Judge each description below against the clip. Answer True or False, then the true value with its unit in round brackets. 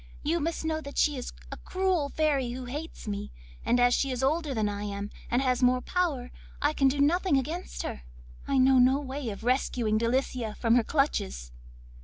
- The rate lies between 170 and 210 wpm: True (200 wpm)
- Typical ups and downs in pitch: True (3.5 semitones)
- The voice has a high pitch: True (260 Hz)